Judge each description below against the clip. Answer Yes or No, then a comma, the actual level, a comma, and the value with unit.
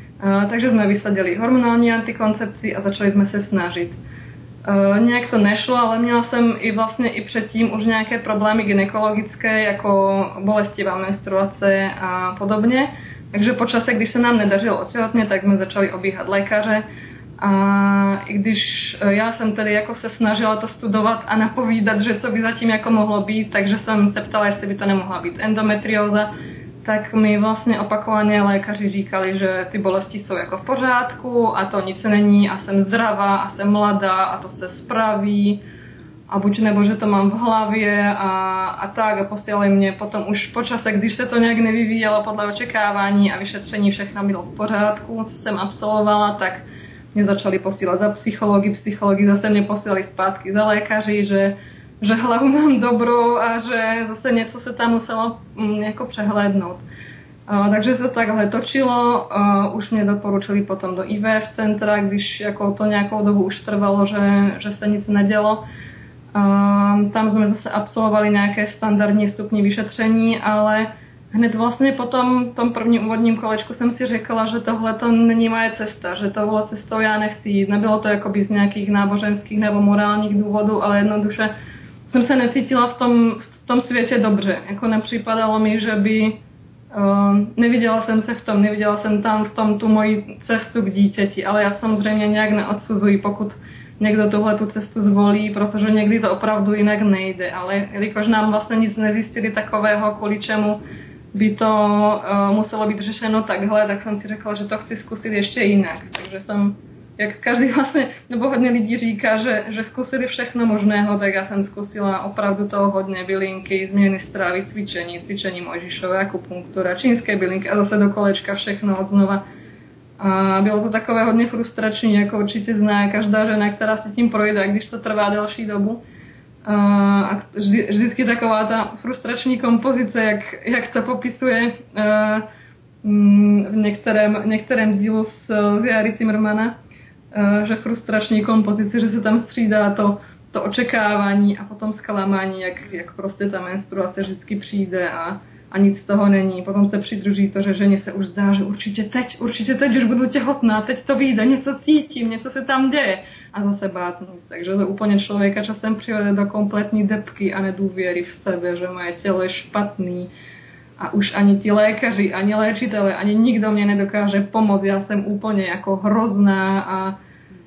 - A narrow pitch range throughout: Yes, narrow, 1.8 semitones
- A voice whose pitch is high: Yes, high, 210 Hz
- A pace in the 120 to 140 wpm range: No, average, 165 wpm